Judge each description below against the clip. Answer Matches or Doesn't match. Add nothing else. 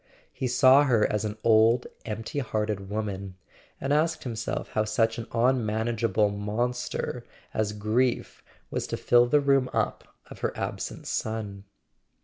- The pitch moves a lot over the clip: Doesn't match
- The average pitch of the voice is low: Matches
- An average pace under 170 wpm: Matches